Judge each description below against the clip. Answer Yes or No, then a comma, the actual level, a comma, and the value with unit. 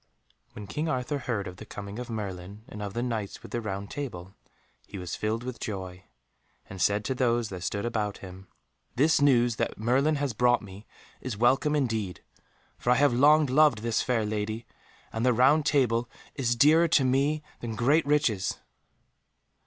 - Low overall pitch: Yes, low, 120 Hz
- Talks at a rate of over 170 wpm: Yes, average, 180 wpm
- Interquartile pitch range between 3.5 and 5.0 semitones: Yes, average, 4.5 semitones